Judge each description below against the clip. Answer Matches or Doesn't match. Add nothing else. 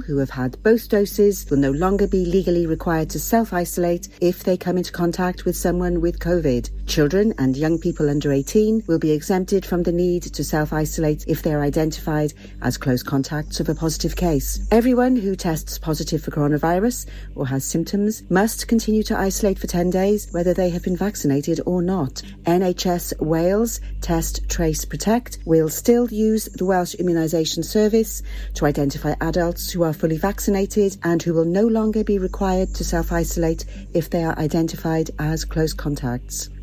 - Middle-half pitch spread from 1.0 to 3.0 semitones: Doesn't match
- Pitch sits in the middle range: Matches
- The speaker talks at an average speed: Matches